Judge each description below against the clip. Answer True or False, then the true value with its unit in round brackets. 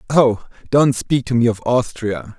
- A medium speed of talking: True (175 wpm)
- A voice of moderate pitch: False (120 Hz)